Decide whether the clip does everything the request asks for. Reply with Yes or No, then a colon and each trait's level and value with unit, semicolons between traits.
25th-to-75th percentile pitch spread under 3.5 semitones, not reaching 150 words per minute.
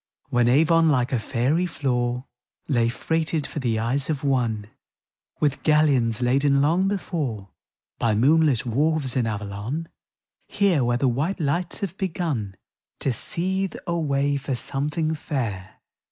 No: average, 4.7 semitones; average, 140 wpm